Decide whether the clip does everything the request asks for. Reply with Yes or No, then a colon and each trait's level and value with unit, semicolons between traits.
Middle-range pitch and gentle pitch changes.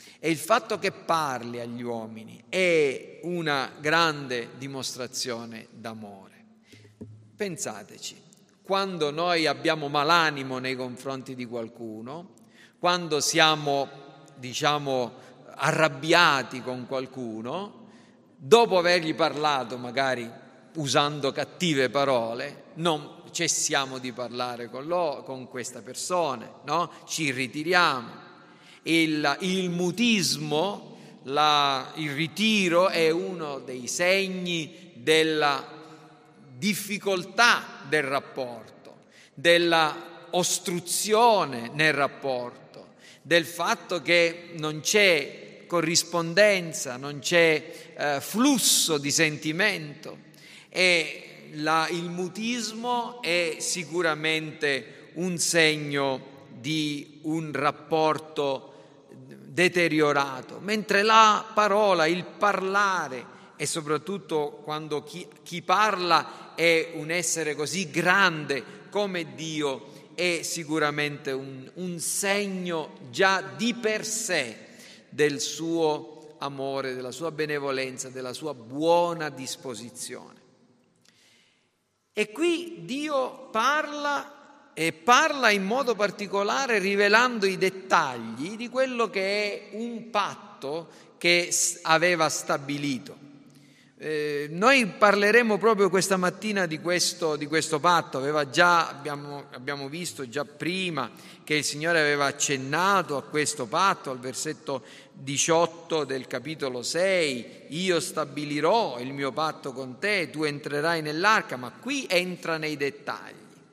No: medium, 160 Hz; average, 4.5 semitones